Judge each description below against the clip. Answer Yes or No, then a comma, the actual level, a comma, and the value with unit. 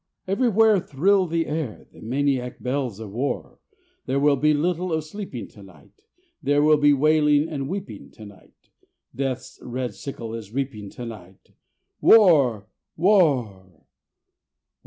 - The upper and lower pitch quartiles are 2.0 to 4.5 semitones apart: No, average, 5.3 semitones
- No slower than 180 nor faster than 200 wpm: No, slow, 135 wpm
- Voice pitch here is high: No, medium, 140 Hz